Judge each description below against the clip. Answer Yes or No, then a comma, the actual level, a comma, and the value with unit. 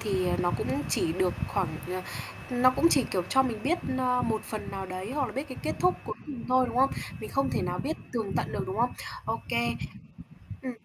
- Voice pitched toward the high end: Yes, high, 230 Hz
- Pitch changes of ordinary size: No, wide, 5.7 semitones